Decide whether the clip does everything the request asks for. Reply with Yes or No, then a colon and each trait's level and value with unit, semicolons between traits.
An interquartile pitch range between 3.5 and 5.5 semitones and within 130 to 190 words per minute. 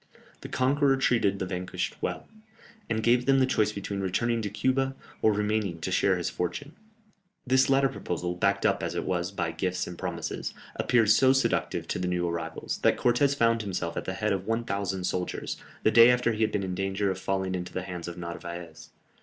No: average, 4.6 semitones; fast, 205 wpm